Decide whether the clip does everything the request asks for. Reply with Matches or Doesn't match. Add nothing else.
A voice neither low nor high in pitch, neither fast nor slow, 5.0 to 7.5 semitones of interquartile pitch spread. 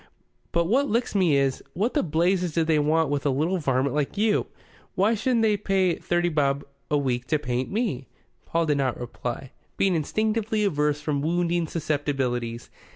Matches